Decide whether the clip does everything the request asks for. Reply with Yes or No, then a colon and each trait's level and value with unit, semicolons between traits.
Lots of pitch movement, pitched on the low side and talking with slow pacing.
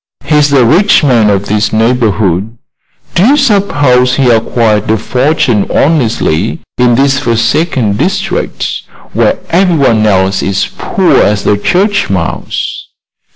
Yes: wide, 6.0 semitones; low, 120 Hz; slow, 130 wpm